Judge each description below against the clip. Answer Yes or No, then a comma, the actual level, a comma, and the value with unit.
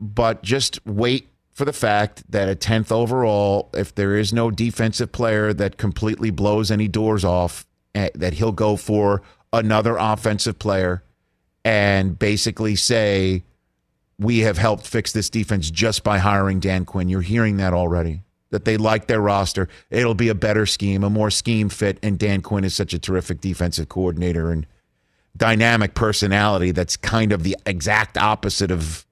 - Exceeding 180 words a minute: No, average, 165 wpm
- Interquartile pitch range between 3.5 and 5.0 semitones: No, average, 2.7 semitones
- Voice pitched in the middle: No, low, 105 Hz